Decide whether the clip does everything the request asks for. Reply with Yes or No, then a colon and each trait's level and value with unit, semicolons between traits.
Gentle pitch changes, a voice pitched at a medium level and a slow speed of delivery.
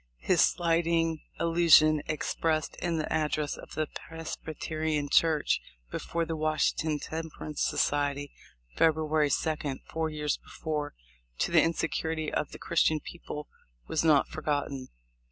Yes: narrow, 1.4 semitones; medium, 155 Hz; slow, 125 wpm